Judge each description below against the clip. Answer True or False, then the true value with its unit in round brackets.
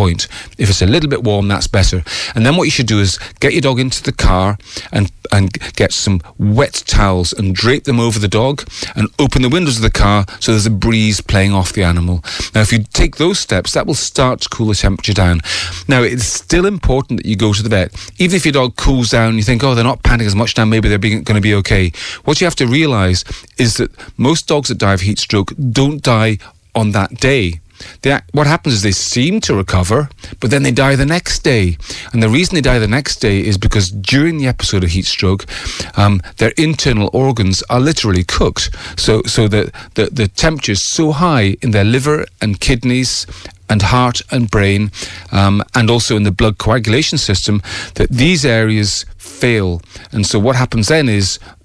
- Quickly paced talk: True (215 wpm)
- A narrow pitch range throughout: False (4.6 semitones)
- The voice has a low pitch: True (110 Hz)